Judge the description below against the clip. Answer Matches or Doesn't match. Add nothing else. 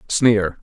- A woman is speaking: Doesn't match